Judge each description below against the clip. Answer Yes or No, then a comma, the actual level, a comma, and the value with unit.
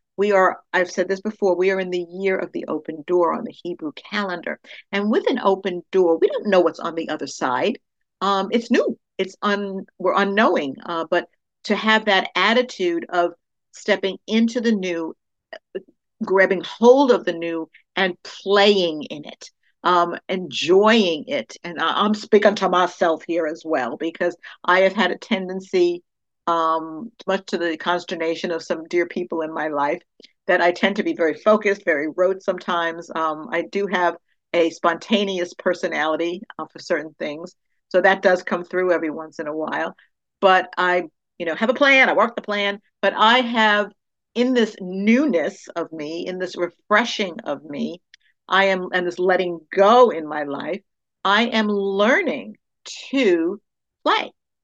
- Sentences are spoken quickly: No, average, 175 wpm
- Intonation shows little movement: No, average, 3.2 semitones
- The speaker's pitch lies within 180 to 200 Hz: Yes, medium, 185 Hz